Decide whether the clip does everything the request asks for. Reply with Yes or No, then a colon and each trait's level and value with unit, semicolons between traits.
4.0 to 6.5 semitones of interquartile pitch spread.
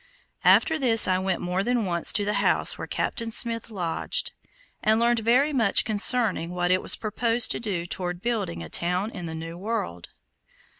Yes: average, 4.6 semitones